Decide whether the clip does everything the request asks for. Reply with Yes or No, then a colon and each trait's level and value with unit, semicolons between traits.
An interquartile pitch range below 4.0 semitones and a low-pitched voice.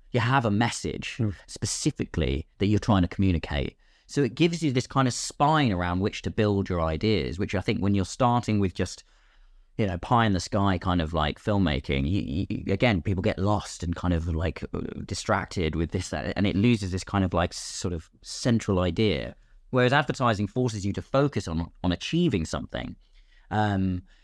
No: average, 4.3 semitones; low, 100 Hz